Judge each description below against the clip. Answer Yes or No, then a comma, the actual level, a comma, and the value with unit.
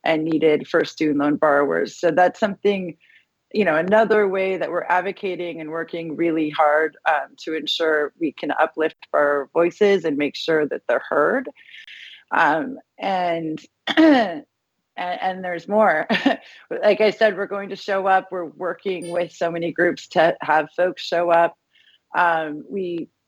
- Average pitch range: Yes, average, 3.5 semitones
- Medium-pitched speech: Yes, medium, 175 Hz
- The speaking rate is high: No, average, 155 wpm